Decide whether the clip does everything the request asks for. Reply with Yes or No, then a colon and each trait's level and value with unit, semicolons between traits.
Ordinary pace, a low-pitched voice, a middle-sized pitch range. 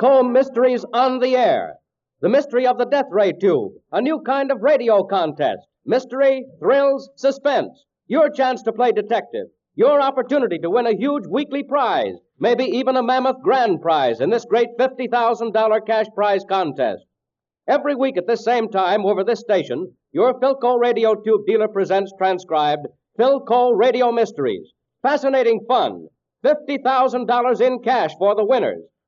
No: average, 155 wpm; very high, 250 Hz; average, 3.6 semitones